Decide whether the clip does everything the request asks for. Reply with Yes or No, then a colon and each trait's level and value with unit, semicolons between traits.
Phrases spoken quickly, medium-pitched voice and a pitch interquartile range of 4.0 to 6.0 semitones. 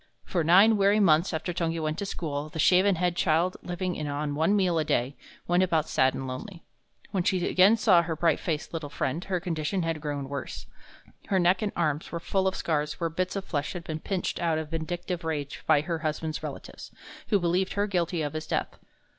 No: fast, 215 wpm; medium, 170 Hz; average, 2.9 semitones